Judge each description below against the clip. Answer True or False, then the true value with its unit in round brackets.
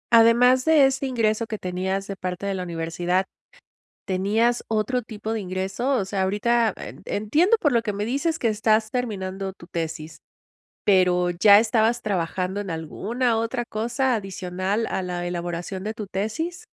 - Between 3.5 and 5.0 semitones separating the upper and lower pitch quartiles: True (3.9 semitones)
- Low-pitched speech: False (210 Hz)